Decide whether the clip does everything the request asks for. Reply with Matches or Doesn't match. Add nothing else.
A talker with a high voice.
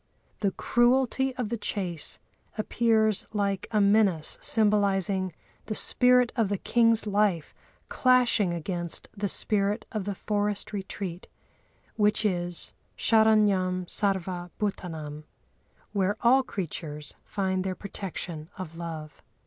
Matches